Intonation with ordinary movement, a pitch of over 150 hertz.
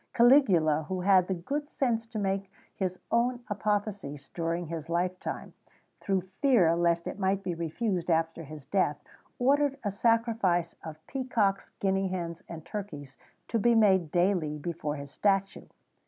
Yes: average, 4.3 semitones; high, 190 Hz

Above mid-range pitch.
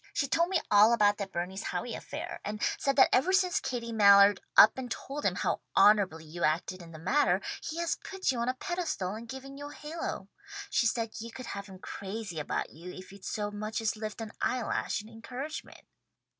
Yes: high, 220 Hz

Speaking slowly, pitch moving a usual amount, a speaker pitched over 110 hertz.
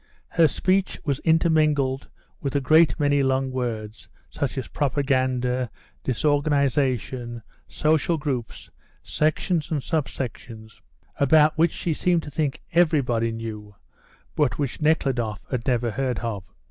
Yes: slow, 125 wpm; average, 4.1 semitones; low, 135 Hz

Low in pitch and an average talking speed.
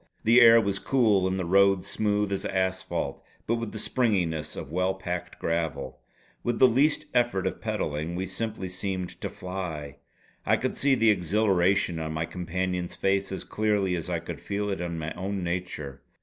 Yes: very low, 95 Hz; average, 180 wpm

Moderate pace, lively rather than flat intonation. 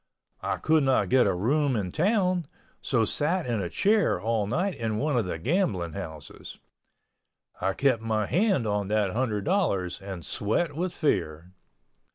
Yes: average, 165 wpm; wide, 7.9 semitones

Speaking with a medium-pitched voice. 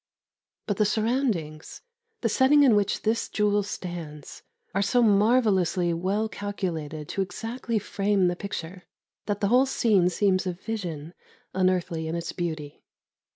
No: high, 195 Hz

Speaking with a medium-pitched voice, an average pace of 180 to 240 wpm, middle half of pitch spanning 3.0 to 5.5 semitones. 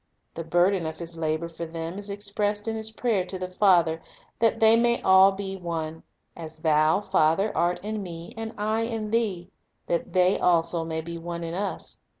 Yes: medium, 180 Hz; average, 185 wpm; average, 3.8 semitones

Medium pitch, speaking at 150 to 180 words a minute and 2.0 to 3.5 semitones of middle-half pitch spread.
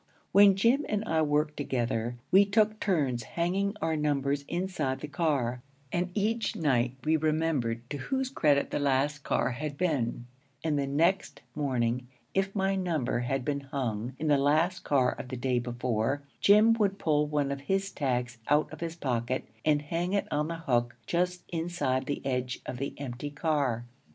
No: medium, 145 Hz; average, 175 wpm; average, 5.3 semitones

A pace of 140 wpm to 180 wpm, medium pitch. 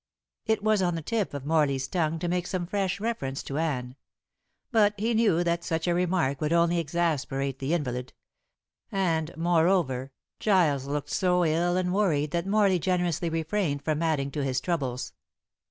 Yes: average, 170 wpm; medium, 170 Hz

